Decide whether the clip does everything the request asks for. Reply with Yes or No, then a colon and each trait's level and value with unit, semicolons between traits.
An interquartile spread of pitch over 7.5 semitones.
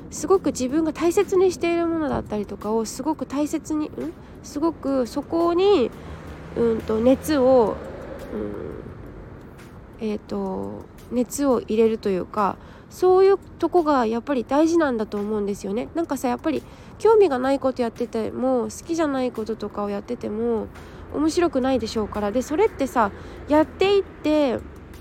No: wide, 6.3 semitones